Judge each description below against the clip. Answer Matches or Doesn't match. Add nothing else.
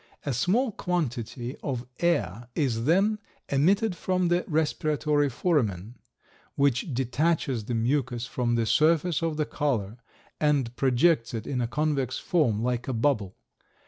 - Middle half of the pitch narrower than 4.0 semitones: Doesn't match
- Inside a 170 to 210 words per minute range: Doesn't match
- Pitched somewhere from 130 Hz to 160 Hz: Matches